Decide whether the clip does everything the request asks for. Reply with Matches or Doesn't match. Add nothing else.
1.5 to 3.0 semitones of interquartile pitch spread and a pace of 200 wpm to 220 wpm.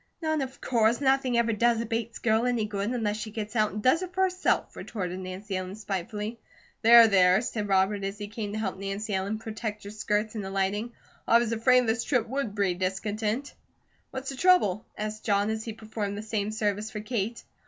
Matches